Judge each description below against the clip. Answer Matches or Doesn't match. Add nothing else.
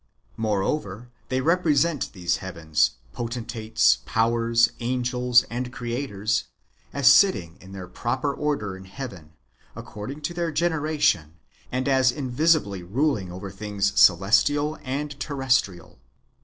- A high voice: Doesn't match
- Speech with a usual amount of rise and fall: Doesn't match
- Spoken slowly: Matches